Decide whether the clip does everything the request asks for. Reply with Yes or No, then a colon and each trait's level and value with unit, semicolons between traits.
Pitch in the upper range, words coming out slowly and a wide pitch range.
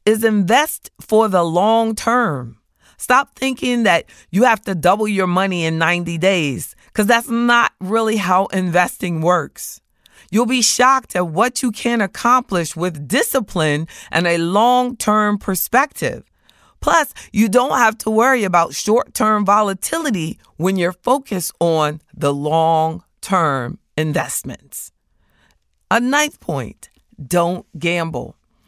Yes: high, 195 Hz; slow, 130 wpm; wide, 5.8 semitones